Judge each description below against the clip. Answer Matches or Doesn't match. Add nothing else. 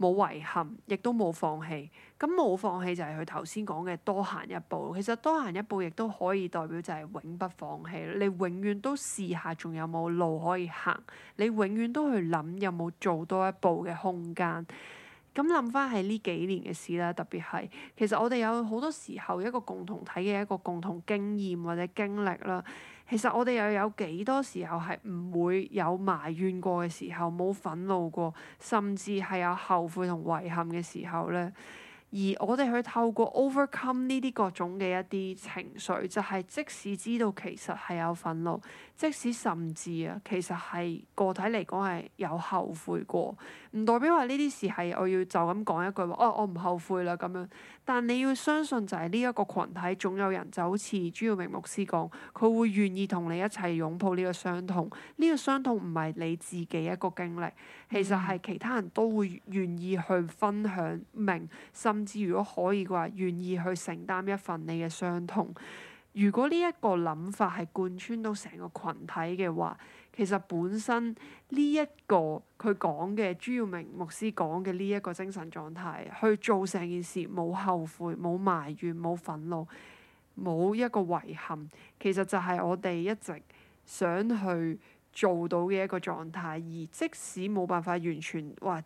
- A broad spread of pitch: Doesn't match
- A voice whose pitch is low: Doesn't match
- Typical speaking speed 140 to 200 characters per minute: Doesn't match